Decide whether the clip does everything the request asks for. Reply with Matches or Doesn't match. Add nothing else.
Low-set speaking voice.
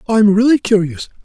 Doesn't match